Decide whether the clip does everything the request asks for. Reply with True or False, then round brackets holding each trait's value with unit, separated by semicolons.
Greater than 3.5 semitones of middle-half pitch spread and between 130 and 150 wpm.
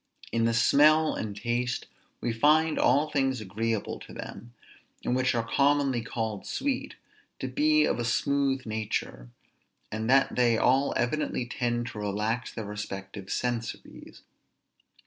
True (3.9 semitones; 140 wpm)